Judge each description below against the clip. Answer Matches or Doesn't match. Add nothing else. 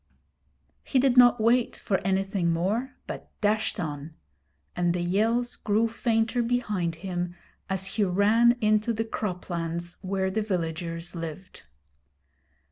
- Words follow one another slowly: Matches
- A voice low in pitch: Doesn't match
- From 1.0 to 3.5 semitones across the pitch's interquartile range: Doesn't match